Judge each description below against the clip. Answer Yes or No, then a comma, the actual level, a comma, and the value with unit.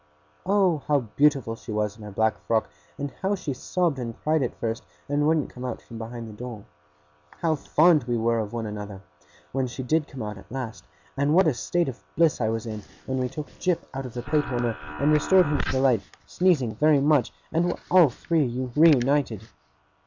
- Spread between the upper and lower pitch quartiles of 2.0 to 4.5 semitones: No, average, 5.0 semitones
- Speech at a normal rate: No, fast, 210 wpm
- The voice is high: No, low, 130 Hz